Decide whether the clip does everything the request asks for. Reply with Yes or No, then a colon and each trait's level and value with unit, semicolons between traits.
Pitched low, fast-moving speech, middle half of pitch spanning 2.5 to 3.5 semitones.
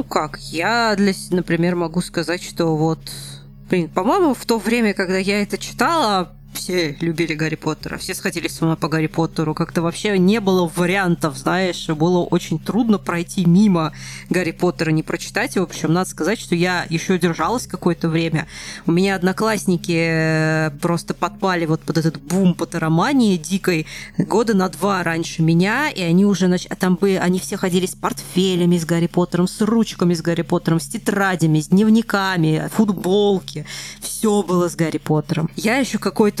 No: medium, 175 Hz; fast, 170 wpm; average, 2.9 semitones